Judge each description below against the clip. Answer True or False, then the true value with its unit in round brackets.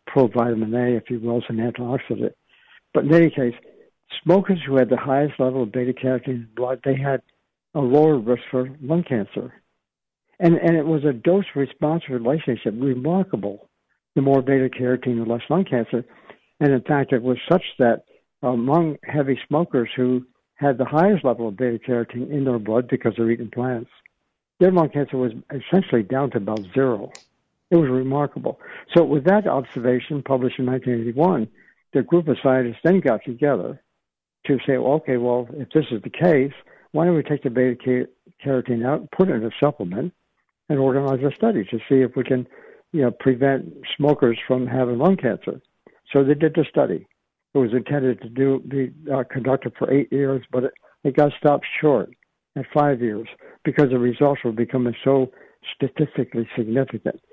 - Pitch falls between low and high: False (130 Hz)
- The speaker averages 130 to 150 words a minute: False (175 wpm)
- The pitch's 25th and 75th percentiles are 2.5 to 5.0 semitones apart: True (3.0 semitones)